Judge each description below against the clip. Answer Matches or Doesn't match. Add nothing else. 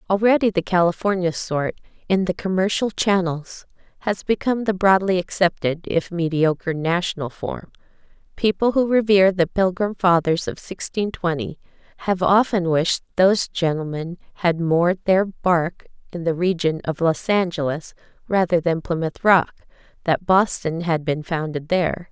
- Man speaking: Doesn't match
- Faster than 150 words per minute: Doesn't match